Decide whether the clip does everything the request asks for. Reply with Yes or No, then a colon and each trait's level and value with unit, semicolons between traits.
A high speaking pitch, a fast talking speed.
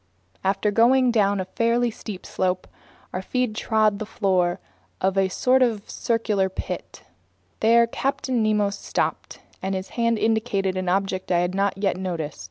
No: high, 200 Hz; average, 160 wpm